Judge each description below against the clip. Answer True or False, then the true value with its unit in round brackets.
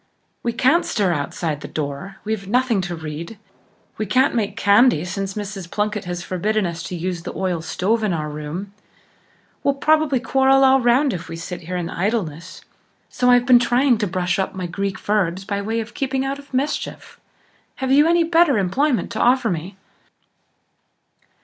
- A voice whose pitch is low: False (205 Hz)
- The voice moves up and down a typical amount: False (6.2 semitones)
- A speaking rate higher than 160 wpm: True (180 wpm)